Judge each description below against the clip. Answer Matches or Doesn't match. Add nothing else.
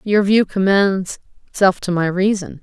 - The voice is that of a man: Doesn't match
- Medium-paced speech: Matches